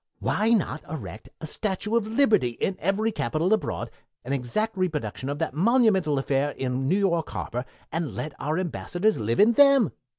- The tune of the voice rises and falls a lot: Yes, wide, 7.5 semitones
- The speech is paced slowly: No, average, 170 wpm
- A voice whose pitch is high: No, medium, 170 Hz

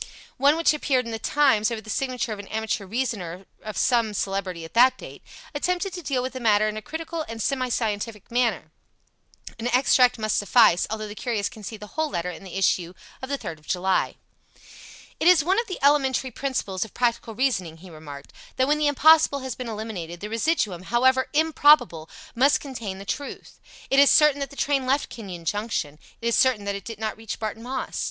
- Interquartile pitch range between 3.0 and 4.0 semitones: No, average, 5.1 semitones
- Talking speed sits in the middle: No, fast, 210 wpm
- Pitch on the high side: Yes, high, 230 Hz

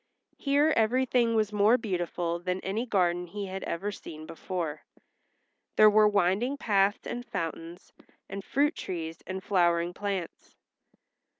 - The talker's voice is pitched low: No, high, 195 Hz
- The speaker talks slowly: Yes, slow, 130 wpm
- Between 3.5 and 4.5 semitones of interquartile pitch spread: Yes, average, 3.8 semitones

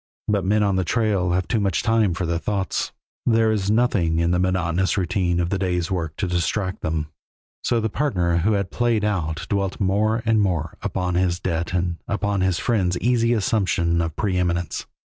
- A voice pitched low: Yes, very low, 95 Hz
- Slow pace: No, average, 190 wpm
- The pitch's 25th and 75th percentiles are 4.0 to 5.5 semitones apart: No, average, 3.3 semitones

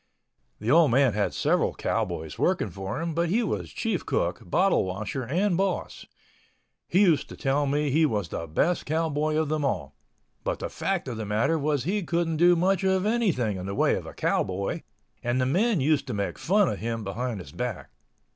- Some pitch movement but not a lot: No, wide, 8.2 semitones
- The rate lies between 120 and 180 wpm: No, fast, 205 wpm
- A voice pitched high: No, medium, 145 Hz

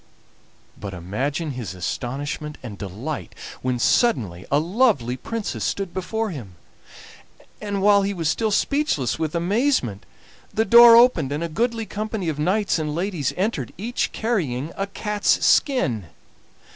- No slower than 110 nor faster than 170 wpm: Yes, average, 140 wpm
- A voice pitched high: No, medium, 170 Hz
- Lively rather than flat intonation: Yes, wide, 8.9 semitones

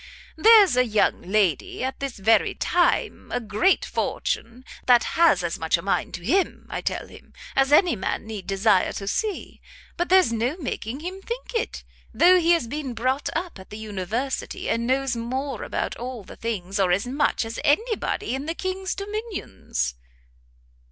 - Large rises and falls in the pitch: Yes, wide, 8.3 semitones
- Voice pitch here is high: Yes, very high, 255 Hz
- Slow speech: No, average, 180 wpm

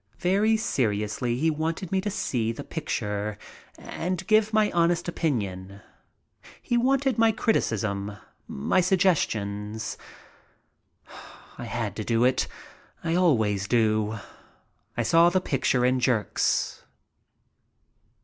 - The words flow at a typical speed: No, slow, 115 wpm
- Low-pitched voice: Yes, low, 130 Hz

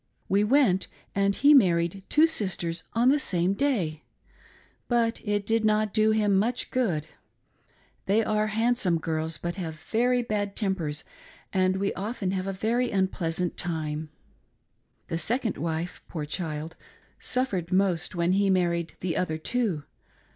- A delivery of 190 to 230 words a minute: No, average, 145 wpm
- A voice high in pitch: Yes, high, 195 Hz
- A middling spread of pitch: Yes, average, 4.5 semitones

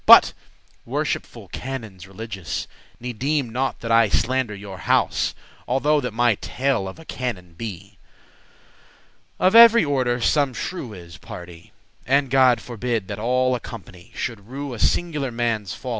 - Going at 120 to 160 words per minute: Yes, average, 150 wpm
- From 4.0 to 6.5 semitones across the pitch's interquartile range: Yes, average, 4.7 semitones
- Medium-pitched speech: No, low, 120 Hz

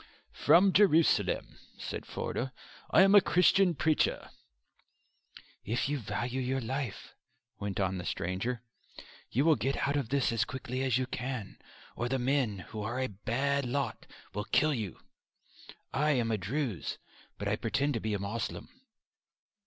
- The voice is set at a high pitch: No, low, 130 Hz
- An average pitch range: Yes, average, 4.4 semitones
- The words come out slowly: No, average, 155 wpm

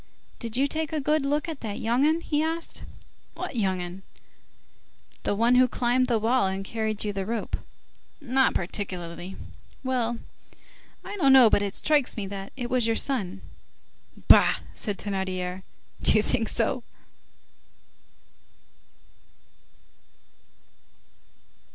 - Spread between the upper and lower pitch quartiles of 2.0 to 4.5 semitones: No, average, 5.2 semitones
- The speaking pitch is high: Yes, high, 230 Hz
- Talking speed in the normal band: No, slow, 130 wpm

